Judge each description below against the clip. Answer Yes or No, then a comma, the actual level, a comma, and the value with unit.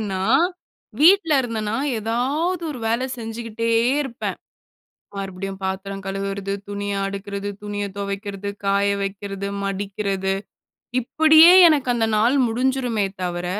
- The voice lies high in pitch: Yes, high, 205 Hz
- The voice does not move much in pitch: No, average, 3.6 semitones